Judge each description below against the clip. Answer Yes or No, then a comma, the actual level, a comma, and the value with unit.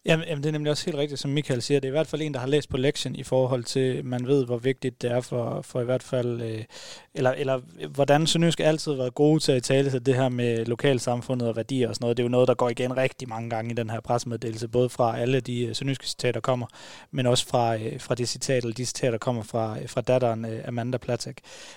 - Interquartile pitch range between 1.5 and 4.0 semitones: Yes, narrow, 2.4 semitones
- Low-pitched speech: Yes, low, 125 Hz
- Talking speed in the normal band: No, fast, 255 wpm